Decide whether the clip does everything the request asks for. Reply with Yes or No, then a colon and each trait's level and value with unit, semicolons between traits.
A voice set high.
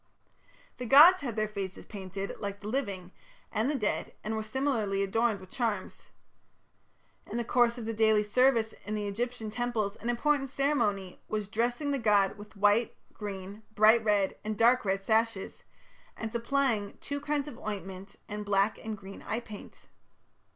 Yes: high, 220 Hz